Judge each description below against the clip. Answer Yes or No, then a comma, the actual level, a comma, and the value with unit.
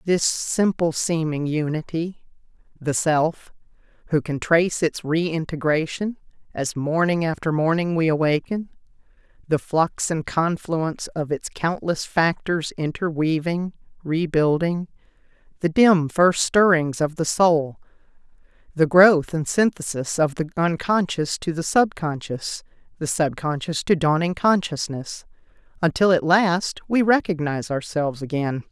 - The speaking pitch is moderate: Yes, medium, 165 Hz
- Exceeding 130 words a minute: No, slow, 115 wpm